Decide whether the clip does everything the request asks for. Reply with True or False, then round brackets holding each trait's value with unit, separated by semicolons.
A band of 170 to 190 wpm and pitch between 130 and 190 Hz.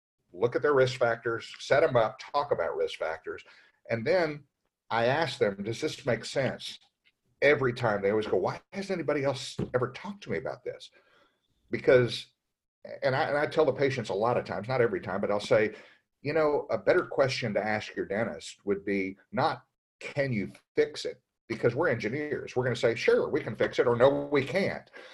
False (205 wpm; 135 Hz)